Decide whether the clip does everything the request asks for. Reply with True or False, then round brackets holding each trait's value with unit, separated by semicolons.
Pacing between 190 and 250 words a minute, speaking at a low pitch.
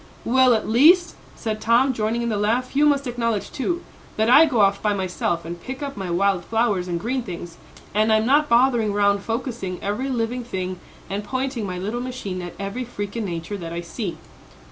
False (205 wpm; 220 Hz)